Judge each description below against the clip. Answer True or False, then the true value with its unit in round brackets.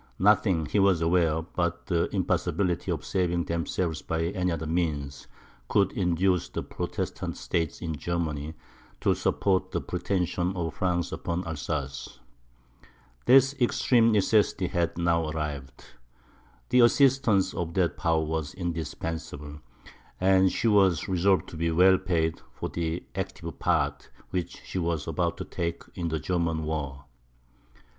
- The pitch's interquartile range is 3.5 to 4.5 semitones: False (2.6 semitones)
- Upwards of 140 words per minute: False (135 wpm)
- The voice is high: False (85 Hz)